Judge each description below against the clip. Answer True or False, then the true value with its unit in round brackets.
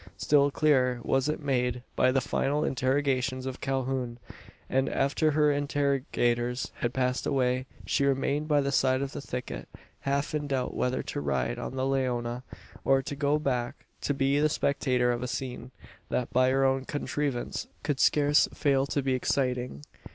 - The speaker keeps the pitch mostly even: True (2.0 semitones)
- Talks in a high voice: False (135 Hz)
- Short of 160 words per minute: False (170 wpm)